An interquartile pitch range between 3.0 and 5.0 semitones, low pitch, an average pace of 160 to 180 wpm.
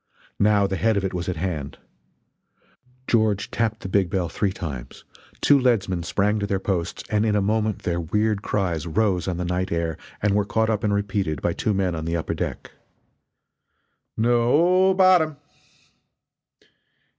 Yes: average, 3.5 semitones; low, 100 Hz; average, 170 wpm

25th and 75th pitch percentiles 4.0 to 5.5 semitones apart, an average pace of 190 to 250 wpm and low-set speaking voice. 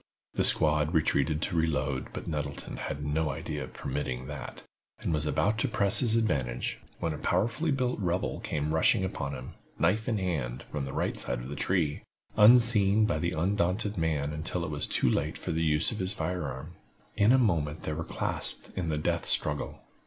Yes: average, 5.2 semitones; average, 195 wpm; very low, 80 Hz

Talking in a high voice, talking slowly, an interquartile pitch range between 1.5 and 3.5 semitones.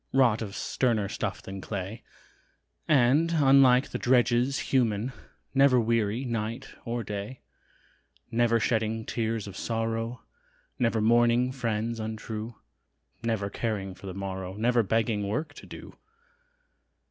No: low, 115 Hz; slow, 125 wpm; narrow, 2.5 semitones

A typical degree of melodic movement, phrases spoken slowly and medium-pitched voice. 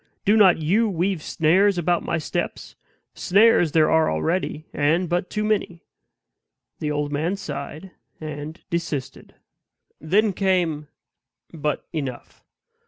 Yes: average, 3.9 semitones; slow, 120 wpm; medium, 165 Hz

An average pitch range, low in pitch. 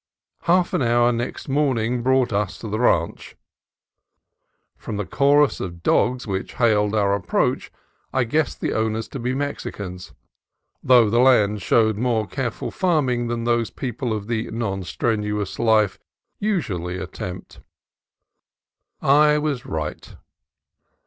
Yes: average, 3.8 semitones; low, 115 Hz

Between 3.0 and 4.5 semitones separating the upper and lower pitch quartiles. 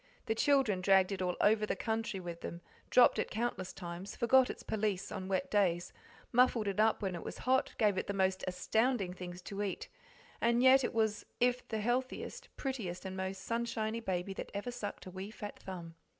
Yes: average, 3.9 semitones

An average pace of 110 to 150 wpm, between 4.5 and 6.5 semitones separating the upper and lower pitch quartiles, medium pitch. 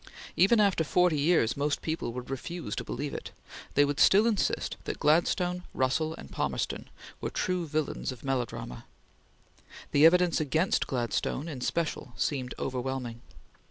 Yes: average, 145 wpm; average, 4.9 semitones; medium, 150 Hz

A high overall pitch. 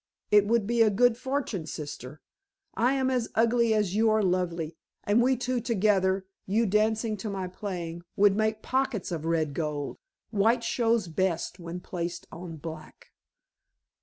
Yes: high, 205 Hz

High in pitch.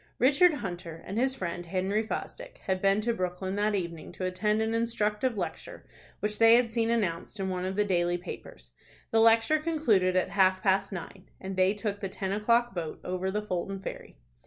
Yes: high, 195 Hz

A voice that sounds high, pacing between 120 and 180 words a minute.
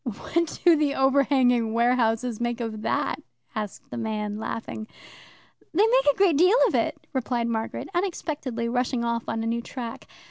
Yes: high, 240 Hz; average, 165 wpm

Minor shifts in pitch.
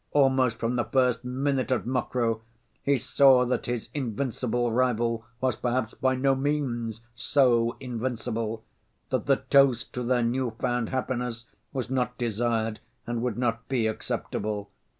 Yes: narrow, 2.0 semitones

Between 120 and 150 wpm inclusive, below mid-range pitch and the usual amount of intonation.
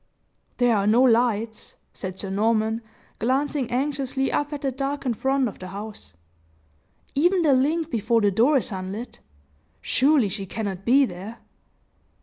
No: average, 145 wpm; high, 240 Hz; average, 4.6 semitones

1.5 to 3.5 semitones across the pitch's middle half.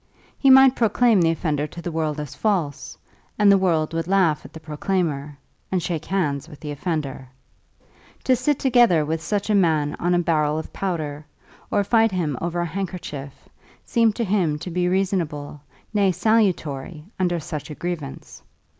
No: average, 4.5 semitones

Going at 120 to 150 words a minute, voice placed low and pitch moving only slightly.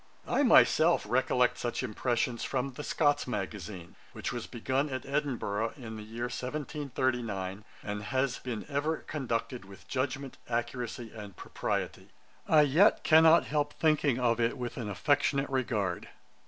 No: average, 140 wpm; low, 125 Hz; average, 4.2 semitones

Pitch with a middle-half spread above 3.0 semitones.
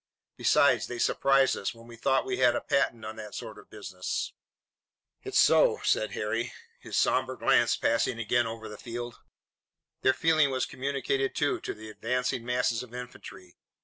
No: average, 2.7 semitones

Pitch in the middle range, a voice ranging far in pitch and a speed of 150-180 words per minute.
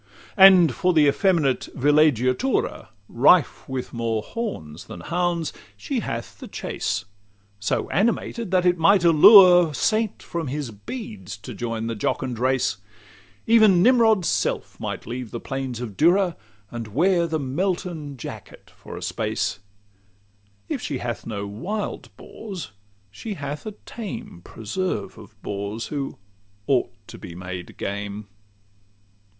No: medium, 150 Hz; wide, 8.3 semitones; slow, 135 wpm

